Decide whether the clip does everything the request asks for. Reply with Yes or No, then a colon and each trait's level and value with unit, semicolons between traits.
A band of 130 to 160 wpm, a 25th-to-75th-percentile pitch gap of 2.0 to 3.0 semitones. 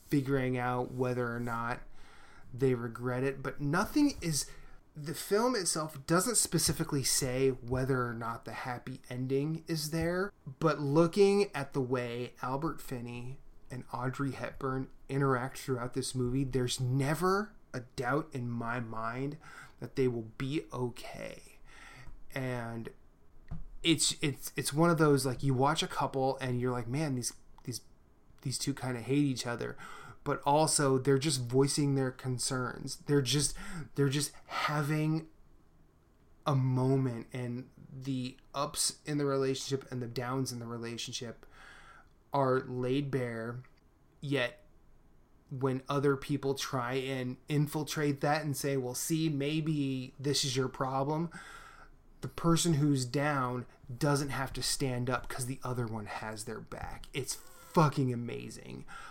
Yes: average, 145 wpm; average, 2.7 semitones